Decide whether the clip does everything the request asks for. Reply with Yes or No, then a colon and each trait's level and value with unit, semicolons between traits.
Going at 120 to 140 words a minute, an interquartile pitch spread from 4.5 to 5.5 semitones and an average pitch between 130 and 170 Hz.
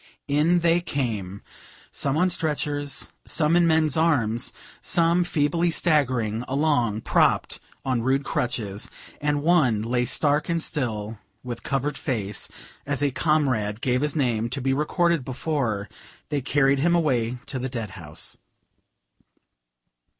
Yes: slow, 135 wpm; average, 4.8 semitones; medium, 140 Hz